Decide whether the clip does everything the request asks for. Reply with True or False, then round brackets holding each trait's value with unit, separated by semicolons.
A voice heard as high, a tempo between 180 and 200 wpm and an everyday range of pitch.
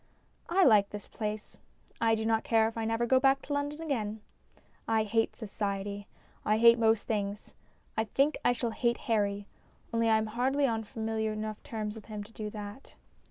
False (220 Hz; 190 wpm; 1.9 semitones)